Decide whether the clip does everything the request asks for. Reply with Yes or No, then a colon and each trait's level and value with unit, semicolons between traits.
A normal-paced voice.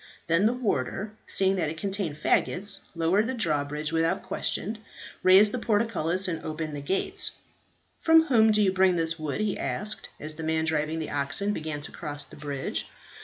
Yes: average, 180 wpm